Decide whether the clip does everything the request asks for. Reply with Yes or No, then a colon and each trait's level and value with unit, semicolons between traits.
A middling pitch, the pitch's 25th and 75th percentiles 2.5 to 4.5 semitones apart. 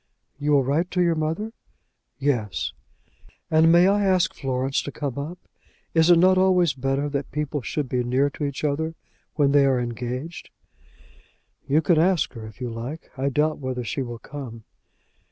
Yes: medium, 145 Hz; average, 3.8 semitones